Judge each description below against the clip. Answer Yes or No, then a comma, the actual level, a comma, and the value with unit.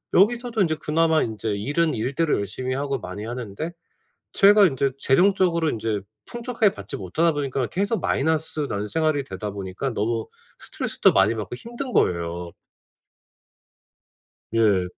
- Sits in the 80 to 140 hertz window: Yes, low, 135 Hz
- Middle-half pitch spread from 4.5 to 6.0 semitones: No, wide, 8.0 semitones